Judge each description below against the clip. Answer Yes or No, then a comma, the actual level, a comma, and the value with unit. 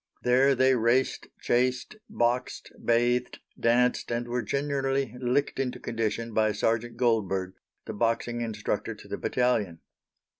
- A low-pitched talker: Yes, low, 120 Hz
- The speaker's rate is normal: No, slow, 125 wpm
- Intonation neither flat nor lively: No, narrow, 1.7 semitones